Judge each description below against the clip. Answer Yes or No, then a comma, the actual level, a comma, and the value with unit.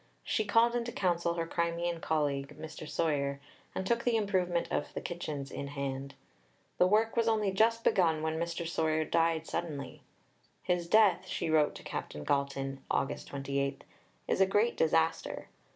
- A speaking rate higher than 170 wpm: No, average, 160 wpm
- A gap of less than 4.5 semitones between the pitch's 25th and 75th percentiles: No, average, 4.8 semitones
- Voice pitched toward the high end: No, medium, 165 Hz